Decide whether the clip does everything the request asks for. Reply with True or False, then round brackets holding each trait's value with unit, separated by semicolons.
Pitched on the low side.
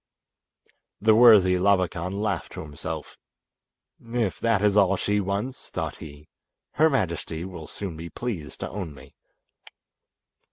True (95 Hz)